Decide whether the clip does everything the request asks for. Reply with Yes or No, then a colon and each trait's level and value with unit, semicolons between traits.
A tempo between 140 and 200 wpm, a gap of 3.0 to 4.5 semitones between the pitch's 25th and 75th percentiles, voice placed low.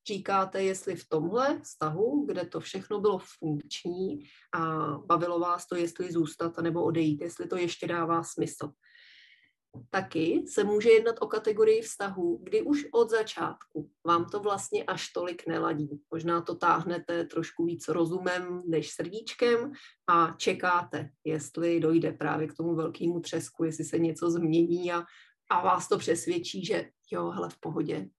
No: average, 150 wpm; average, 3.6 semitones; medium, 170 Hz